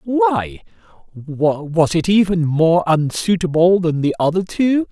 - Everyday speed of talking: No, slow, 120 wpm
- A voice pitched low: No, medium, 170 Hz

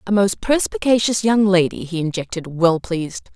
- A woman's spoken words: Yes, female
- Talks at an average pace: Yes, average, 160 wpm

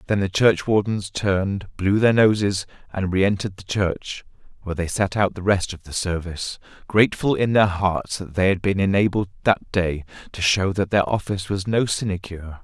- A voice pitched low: Yes, very low, 95 Hz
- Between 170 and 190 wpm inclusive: Yes, average, 185 wpm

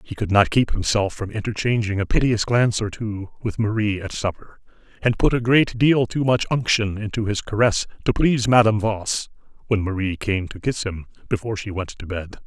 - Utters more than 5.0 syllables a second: Yes, 5.5 syllables/s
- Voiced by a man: Yes, male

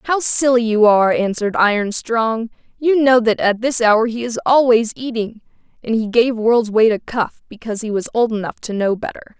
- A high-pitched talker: Yes, high, 230 Hz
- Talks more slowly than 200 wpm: No, fast, 205 wpm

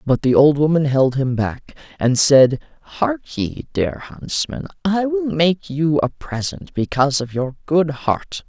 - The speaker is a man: Yes, male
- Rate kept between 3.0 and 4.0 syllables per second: Yes, 3.9 syllables/s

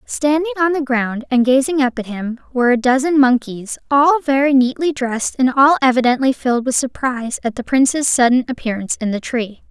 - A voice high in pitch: Yes, very high, 260 Hz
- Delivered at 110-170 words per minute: No, average, 190 wpm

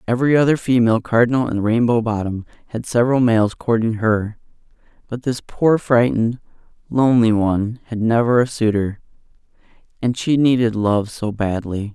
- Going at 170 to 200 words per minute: No, average, 140 wpm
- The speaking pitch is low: Yes, low, 115 Hz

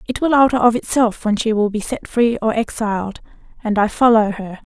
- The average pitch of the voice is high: Yes, high, 225 Hz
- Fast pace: Yes, fast, 215 wpm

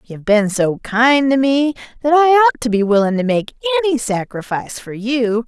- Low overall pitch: No, very high, 250 Hz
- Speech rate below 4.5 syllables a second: No, 5.5 syllables/s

